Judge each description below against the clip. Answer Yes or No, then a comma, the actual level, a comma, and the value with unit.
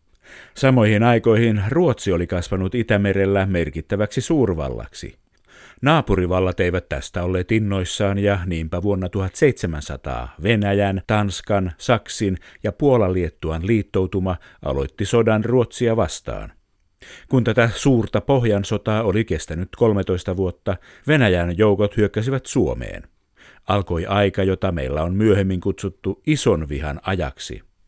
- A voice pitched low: Yes, low, 100 Hz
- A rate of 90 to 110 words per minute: Yes, average, 105 wpm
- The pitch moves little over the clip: No, average, 3.6 semitones